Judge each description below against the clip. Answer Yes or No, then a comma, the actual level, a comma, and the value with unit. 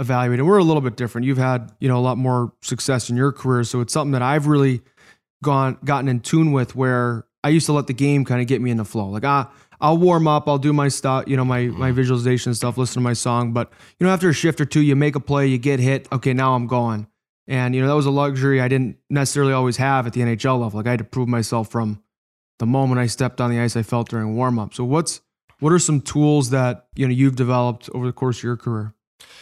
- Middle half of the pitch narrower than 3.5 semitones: Yes, narrow, 2.5 semitones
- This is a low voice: Yes, low, 130 Hz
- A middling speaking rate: No, fast, 270 wpm